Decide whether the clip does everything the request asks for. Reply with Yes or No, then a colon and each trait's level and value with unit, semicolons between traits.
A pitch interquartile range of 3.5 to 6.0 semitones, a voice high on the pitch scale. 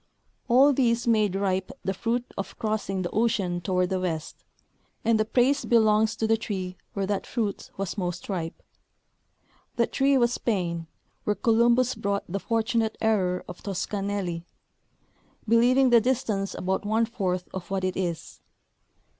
Yes: average, 3.8 semitones; high, 205 Hz